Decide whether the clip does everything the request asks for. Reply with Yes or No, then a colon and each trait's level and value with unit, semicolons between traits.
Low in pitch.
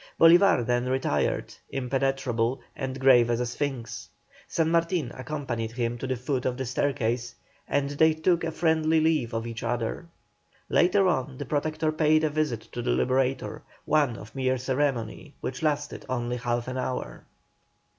Yes: low, 130 Hz